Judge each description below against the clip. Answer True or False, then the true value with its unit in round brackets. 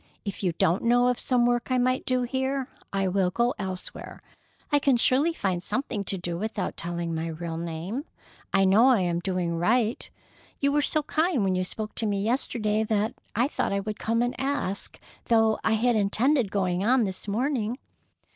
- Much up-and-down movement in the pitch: False (5.0 semitones)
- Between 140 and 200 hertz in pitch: False (220 Hz)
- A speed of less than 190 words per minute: False (195 wpm)